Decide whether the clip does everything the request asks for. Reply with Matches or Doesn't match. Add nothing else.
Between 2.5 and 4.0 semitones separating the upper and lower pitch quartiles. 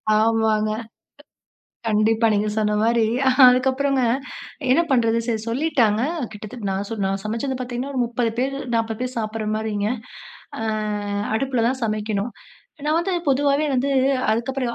Matches